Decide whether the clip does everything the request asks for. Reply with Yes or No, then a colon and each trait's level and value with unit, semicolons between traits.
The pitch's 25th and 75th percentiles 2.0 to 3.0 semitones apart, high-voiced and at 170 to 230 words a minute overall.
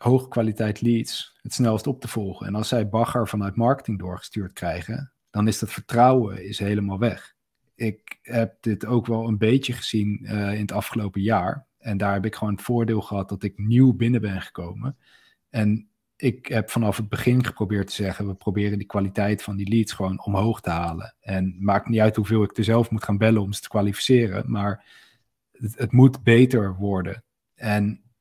No: narrow, 2.5 semitones; low, 110 Hz; average, 195 wpm